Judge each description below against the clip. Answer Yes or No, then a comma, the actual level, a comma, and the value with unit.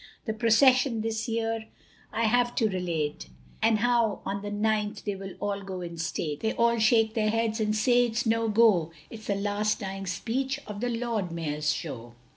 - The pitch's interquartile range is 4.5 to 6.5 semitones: No, average, 2.8 semitones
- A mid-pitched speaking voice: No, high, 215 Hz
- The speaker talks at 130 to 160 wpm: No, average, 190 wpm